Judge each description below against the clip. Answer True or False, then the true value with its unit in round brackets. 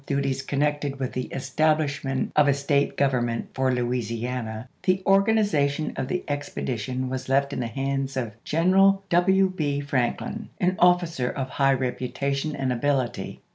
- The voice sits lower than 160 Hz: True (140 Hz)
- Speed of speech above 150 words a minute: False (145 wpm)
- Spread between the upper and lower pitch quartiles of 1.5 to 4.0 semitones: True (3.3 semitones)